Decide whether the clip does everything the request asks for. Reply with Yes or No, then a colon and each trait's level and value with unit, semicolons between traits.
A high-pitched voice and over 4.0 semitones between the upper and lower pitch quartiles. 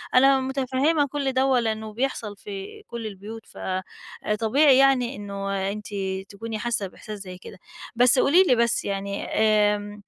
Yes: high, 225 Hz; average, 4.4 semitones